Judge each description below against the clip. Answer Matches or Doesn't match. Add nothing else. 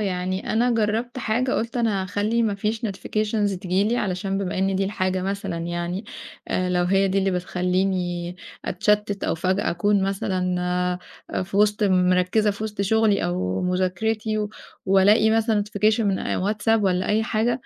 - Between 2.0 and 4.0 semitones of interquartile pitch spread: Matches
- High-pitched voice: Matches